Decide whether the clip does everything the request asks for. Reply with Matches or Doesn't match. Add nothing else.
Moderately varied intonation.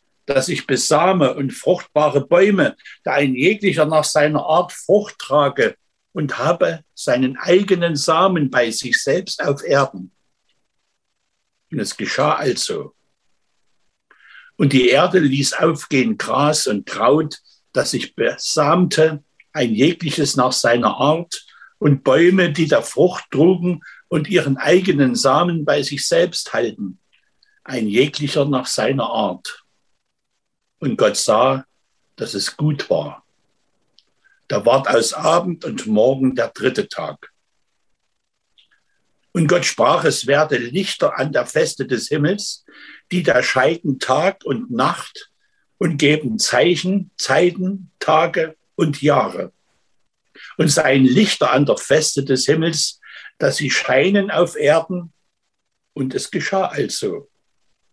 Matches